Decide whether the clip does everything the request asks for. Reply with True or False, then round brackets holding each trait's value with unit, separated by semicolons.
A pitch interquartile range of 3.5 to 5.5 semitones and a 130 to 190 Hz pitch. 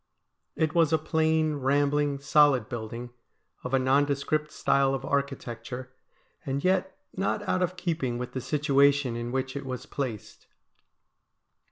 False (2.9 semitones; 140 Hz)